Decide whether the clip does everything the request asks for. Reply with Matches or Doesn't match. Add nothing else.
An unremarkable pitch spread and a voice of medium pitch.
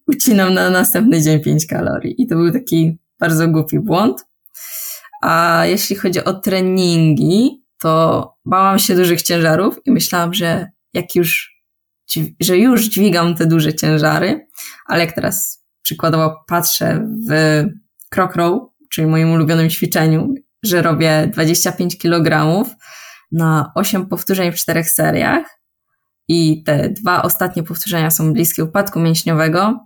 Matches